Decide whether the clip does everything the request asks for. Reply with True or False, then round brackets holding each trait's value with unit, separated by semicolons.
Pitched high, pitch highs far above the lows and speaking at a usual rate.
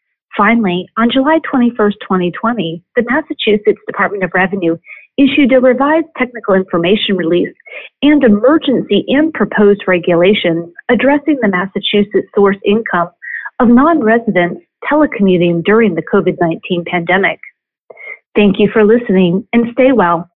False (210 Hz; 5.8 semitones; 120 wpm)